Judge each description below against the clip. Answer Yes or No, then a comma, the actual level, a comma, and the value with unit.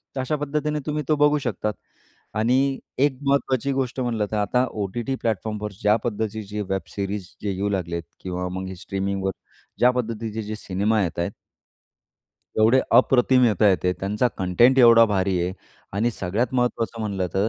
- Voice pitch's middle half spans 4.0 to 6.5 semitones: Yes, average, 4.4 semitones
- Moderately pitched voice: No, low, 110 Hz